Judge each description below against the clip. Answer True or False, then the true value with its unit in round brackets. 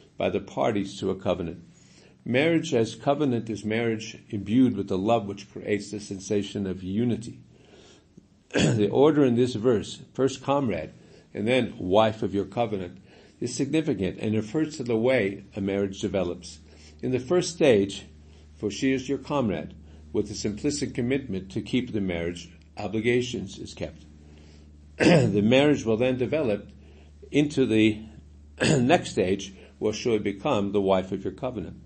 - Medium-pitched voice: False (105 Hz)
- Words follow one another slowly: False (155 wpm)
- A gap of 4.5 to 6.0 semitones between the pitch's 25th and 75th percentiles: True (5.2 semitones)